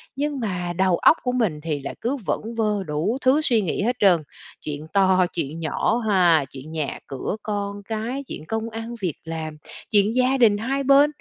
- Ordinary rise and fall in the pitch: No, wide, 6.2 semitones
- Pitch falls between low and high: No, high, 205 Hz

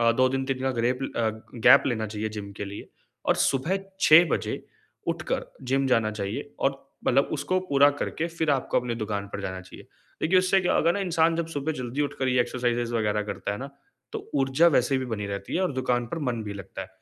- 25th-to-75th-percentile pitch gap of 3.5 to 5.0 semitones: Yes, average, 4.7 semitones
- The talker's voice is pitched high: No, low, 130 Hz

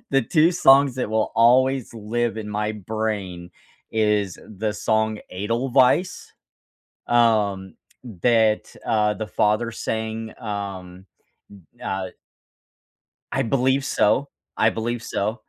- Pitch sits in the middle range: No, low, 110 Hz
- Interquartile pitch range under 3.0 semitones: Yes, narrow, 2.4 semitones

